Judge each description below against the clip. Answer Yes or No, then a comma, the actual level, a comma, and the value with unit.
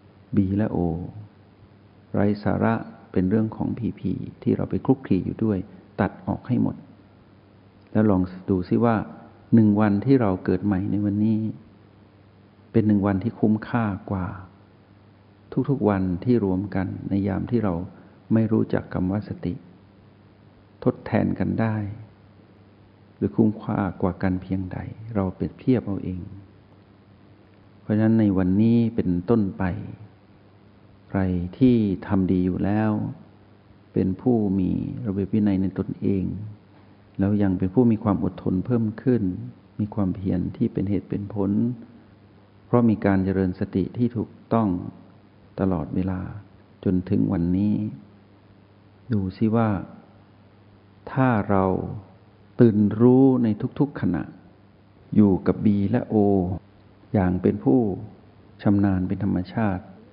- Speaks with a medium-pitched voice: No, low, 100 Hz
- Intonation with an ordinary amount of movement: No, narrow, 1.8 semitones